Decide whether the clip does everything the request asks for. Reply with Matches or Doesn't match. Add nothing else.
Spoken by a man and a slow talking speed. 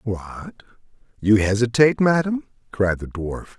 Matches